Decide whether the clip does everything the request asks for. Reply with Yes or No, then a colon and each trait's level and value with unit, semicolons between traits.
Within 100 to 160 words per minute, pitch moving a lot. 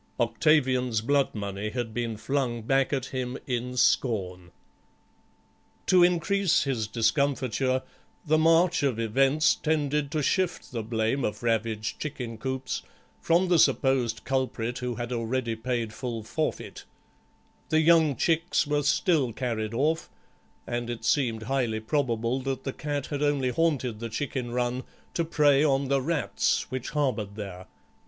No: average, 140 wpm; average, 4.1 semitones